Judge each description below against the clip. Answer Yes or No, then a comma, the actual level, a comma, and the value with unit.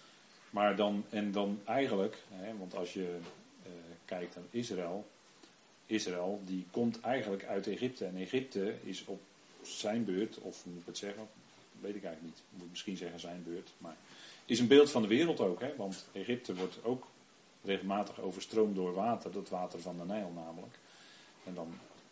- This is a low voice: Yes, very low, 95 Hz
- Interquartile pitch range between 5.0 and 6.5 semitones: No, average, 3.4 semitones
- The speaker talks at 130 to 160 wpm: No, average, 175 wpm